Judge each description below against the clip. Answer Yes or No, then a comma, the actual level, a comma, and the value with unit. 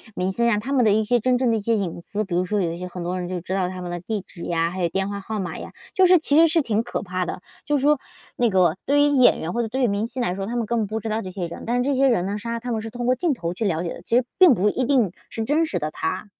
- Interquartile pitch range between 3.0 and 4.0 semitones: No, average, 5.1 semitones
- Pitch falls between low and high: No, high, 215 Hz